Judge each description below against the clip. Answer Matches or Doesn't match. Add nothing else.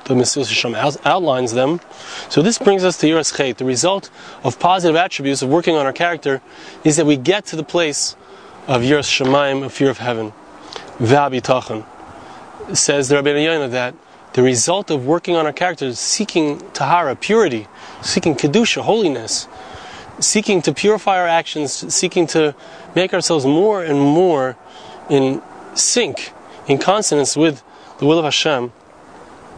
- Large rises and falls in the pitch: Doesn't match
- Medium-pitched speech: Matches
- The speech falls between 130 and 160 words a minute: Matches